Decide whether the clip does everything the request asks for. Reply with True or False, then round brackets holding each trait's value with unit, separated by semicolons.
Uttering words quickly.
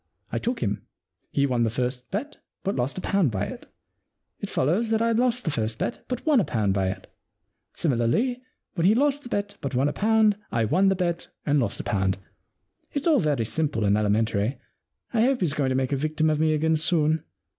True (220 wpm)